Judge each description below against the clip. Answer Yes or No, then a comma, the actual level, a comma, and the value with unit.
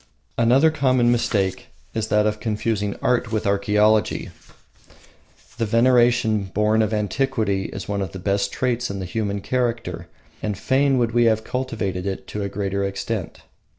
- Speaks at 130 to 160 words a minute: Yes, average, 155 wpm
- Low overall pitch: Yes, low, 110 Hz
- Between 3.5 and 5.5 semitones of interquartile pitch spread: No, average, 3.1 semitones